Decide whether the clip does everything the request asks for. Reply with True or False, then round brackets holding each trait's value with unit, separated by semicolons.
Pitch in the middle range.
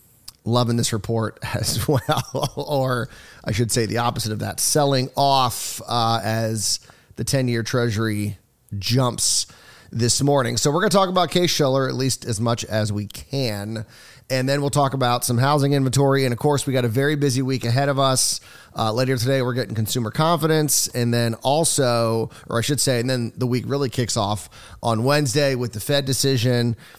False (125 Hz)